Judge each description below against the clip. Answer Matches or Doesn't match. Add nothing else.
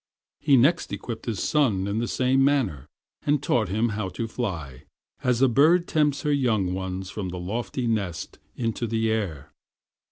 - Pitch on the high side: Doesn't match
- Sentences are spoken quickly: Doesn't match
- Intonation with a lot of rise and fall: Matches